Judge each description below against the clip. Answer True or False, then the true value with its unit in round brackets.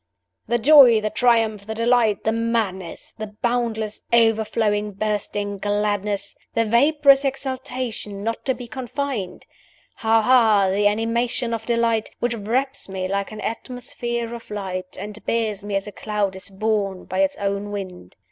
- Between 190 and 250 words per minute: False (150 wpm)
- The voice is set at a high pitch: True (220 Hz)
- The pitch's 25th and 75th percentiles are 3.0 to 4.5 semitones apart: False (2.6 semitones)